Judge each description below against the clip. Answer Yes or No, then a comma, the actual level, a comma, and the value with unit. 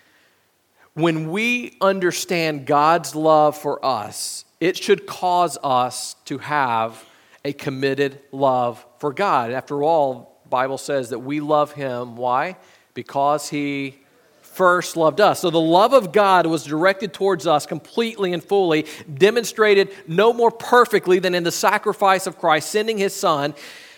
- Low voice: No, medium, 160 Hz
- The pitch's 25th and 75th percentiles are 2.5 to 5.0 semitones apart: No, wide, 5.4 semitones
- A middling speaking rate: Yes, average, 145 wpm